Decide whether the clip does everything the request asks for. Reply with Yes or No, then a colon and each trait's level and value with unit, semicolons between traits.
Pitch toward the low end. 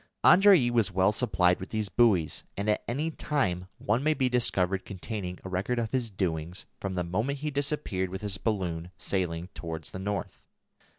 Yes: low, 100 Hz